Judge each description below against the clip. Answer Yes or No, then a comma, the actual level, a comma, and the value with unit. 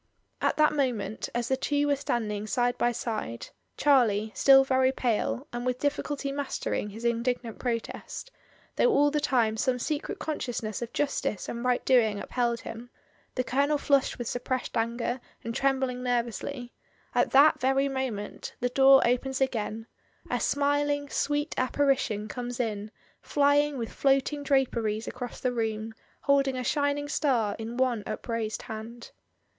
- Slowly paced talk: No, average, 160 wpm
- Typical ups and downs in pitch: Yes, average, 3.3 semitones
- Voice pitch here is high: Yes, very high, 250 Hz